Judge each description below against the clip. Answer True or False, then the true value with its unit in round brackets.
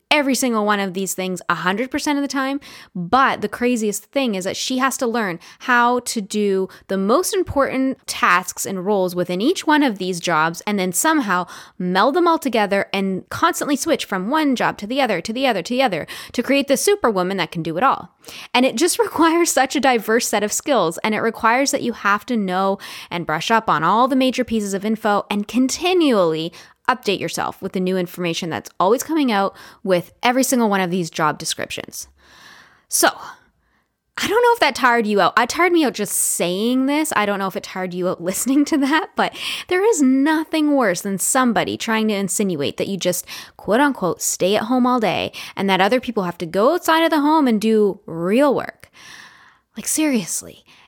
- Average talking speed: False (210 wpm)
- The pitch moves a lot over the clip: True (6.1 semitones)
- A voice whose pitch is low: False (225 Hz)